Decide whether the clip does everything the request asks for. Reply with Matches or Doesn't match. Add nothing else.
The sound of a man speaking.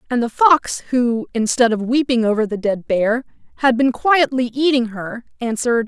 Doesn't match